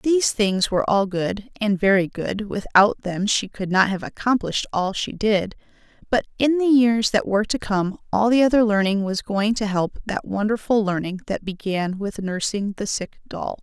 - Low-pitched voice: No, high, 205 Hz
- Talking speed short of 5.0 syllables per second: Yes, 4.8 syllables/s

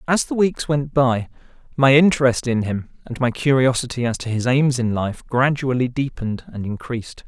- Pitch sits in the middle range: No, low, 130 Hz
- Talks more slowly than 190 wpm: Yes, average, 180 wpm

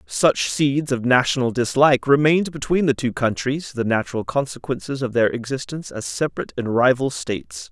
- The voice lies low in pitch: Yes, low, 130 Hz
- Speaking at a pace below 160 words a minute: No, average, 165 wpm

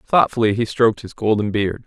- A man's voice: Yes, male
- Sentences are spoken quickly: No, average, 195 wpm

